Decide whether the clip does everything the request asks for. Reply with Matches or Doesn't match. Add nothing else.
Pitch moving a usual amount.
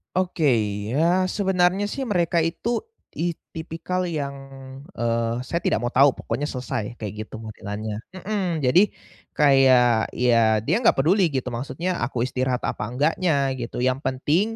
Doesn't match